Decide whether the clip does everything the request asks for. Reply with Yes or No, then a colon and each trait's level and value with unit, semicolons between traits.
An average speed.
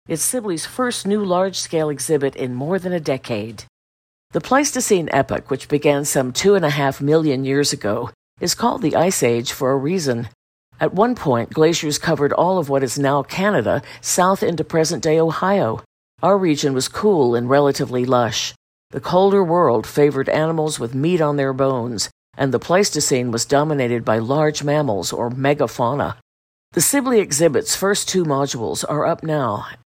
Yes: average, 170 wpm